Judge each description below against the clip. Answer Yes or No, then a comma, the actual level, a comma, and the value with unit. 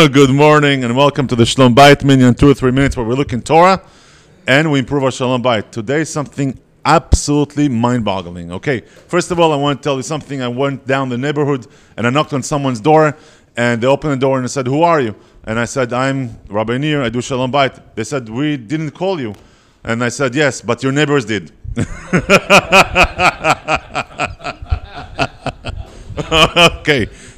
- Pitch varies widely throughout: No, average, 3.4 semitones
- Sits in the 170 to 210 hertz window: No, low, 135 Hz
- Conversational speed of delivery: Yes, average, 190 wpm